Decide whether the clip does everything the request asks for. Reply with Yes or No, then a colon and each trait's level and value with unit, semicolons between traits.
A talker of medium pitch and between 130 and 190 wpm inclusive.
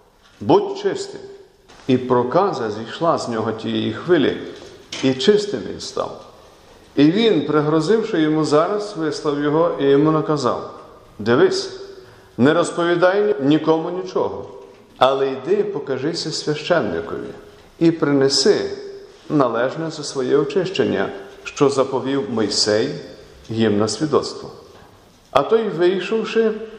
No: medium, 165 Hz; slow, 105 wpm